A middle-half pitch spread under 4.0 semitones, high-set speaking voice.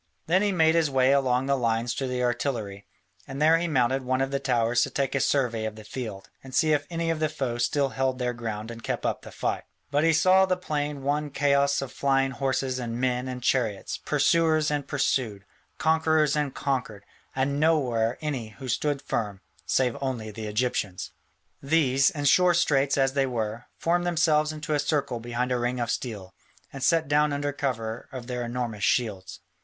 No: average, 3.5 semitones; low, 135 Hz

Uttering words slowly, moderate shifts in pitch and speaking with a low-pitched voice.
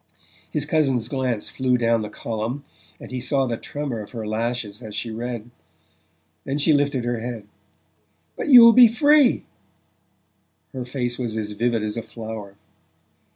No: average, 155 wpm; average, 3.7 semitones; low, 120 Hz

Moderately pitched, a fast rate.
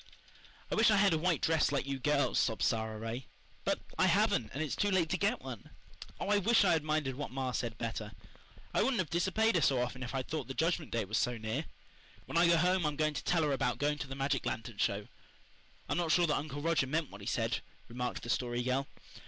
Yes: medium, 145 Hz; fast, 245 wpm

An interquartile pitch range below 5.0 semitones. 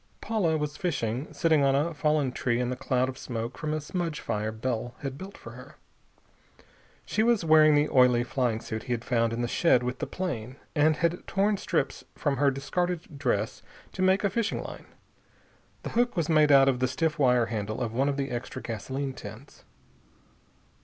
Yes: average, 4.6 semitones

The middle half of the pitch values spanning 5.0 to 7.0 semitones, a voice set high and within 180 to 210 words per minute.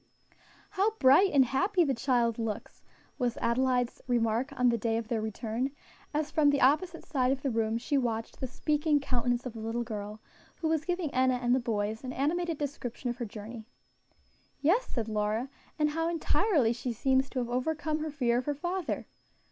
No: average, 4.2 semitones; very high, 255 Hz; average, 190 wpm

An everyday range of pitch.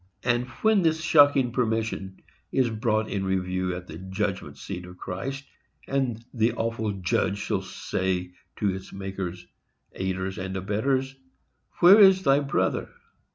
No: wide, 6.0 semitones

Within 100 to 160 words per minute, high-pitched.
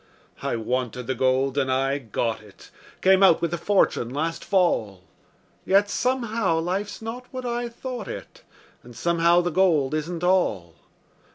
No: average, 155 wpm; medium, 170 Hz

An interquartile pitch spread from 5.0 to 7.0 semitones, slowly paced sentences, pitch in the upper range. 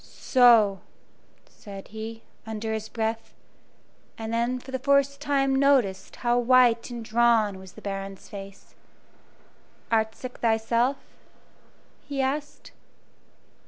No: average, 2.9 semitones; slow, 115 wpm; high, 230 Hz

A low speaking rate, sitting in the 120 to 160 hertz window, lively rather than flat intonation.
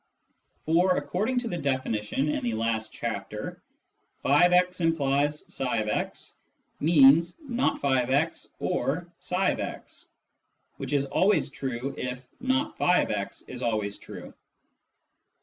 Yes: slow, 115 wpm; medium, 140 Hz; wide, 6.6 semitones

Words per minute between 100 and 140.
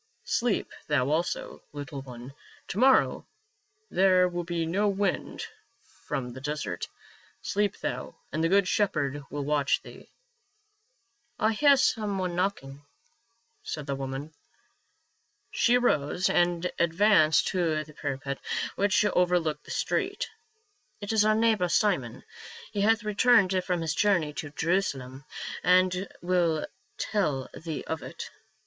Yes: slow, 135 wpm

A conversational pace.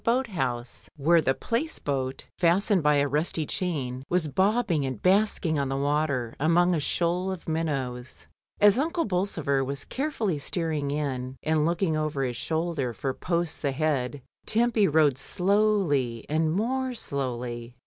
Yes: average, 150 wpm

